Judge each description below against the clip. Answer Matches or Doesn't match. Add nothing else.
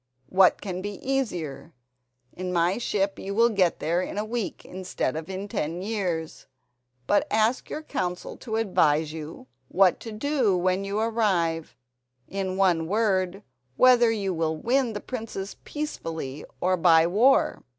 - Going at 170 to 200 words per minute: Doesn't match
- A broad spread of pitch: Doesn't match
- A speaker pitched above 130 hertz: Matches